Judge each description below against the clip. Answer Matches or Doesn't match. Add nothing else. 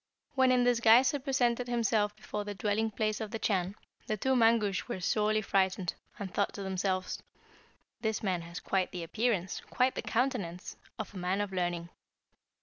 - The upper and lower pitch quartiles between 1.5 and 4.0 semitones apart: Matches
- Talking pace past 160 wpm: Matches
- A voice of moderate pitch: Doesn't match